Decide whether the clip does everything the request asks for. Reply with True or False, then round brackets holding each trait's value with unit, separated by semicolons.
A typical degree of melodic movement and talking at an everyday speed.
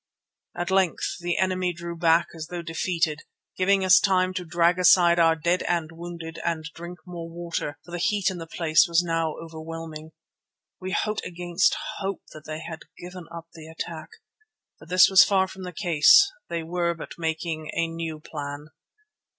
False (1.8 semitones; 175 wpm)